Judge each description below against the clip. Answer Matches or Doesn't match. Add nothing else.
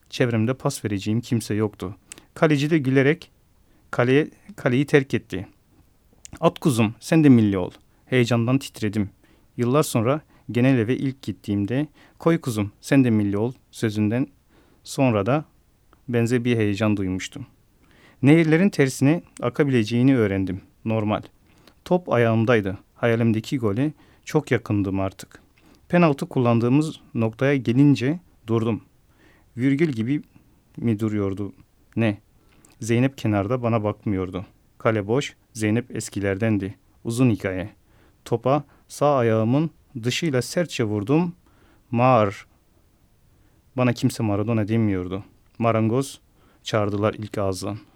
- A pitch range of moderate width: Matches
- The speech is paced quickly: Doesn't match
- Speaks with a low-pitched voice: Matches